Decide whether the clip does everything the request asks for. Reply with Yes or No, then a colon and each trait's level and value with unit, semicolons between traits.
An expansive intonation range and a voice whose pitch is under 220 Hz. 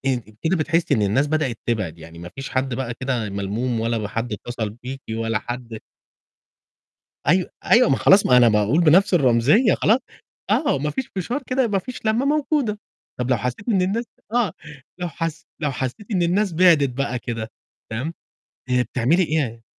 Yes: wide, 7.8 semitones; low, 135 Hz